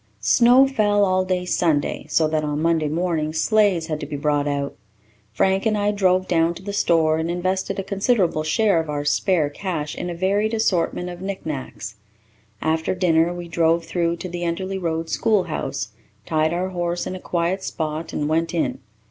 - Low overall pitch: No, medium, 170 Hz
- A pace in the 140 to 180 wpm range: No, average, 190 wpm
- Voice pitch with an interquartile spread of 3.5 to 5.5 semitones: No, average, 3.0 semitones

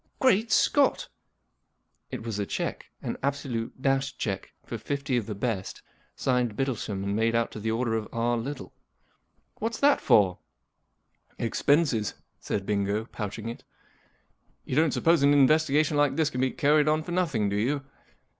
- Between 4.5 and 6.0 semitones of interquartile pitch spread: Yes, average, 4.8 semitones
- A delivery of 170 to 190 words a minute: Yes, average, 175 wpm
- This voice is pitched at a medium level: No, low, 125 Hz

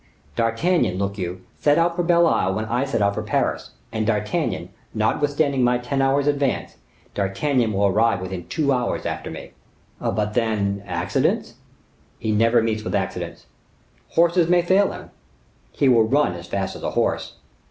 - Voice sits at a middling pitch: No, low, 115 Hz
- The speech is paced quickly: No, average, 165 wpm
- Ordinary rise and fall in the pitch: No, wide, 6.0 semitones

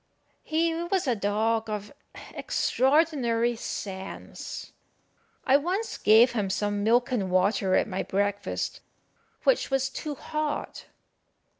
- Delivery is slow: Yes, slow, 115 wpm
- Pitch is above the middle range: Yes, high, 230 Hz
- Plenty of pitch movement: Yes, wide, 6.2 semitones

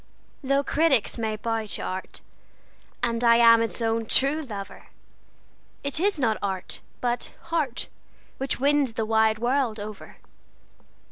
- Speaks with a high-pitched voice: Yes, high, 230 Hz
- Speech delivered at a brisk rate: No, slow, 135 wpm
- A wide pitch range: No, average, 3.8 semitones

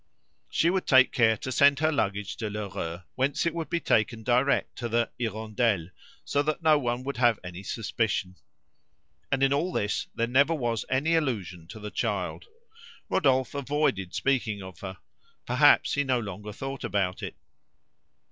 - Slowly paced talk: No, average, 165 wpm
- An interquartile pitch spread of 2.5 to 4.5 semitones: No, average, 5.3 semitones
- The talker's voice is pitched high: No, low, 120 Hz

